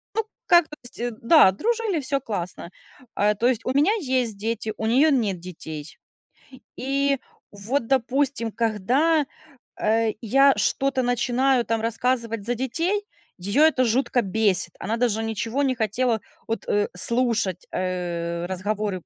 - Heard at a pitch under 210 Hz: No, high, 230 Hz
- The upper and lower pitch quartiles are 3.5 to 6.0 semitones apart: Yes, average, 4.4 semitones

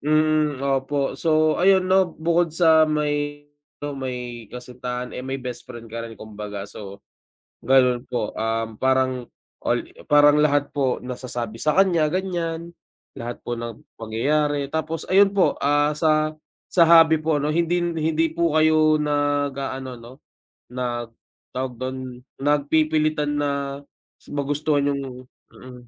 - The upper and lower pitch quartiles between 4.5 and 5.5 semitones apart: No, average, 3.8 semitones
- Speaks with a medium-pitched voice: Yes, medium, 145 Hz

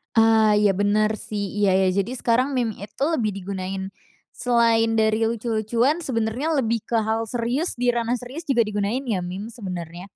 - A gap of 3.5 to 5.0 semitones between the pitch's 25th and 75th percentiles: No, average, 2.9 semitones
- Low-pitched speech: No, high, 225 Hz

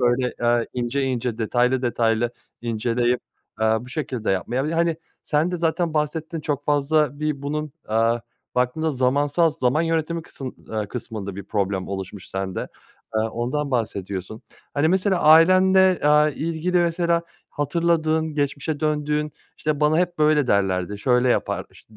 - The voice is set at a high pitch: No, medium, 145 Hz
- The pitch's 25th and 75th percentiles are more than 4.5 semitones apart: Yes, average, 5.0 semitones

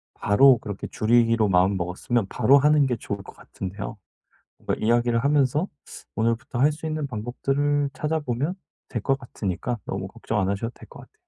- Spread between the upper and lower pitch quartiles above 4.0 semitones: Yes, average, 5.2 semitones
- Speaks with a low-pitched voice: Yes, low, 120 Hz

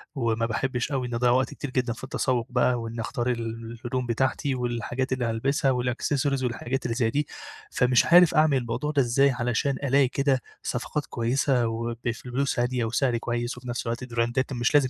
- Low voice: Yes, low, 125 Hz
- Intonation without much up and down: Yes, narrow, 2.1 semitones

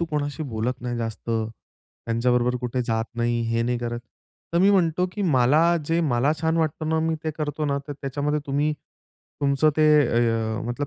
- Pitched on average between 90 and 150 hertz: Yes, medium, 140 Hz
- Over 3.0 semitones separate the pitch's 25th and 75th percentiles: Yes, average, 4.8 semitones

